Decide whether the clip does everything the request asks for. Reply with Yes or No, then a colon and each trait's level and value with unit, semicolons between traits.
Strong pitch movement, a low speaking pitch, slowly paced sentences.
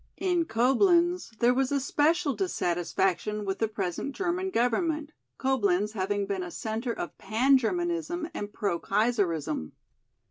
No: wide, 7.9 semitones; high, 235 Hz; slow, 130 wpm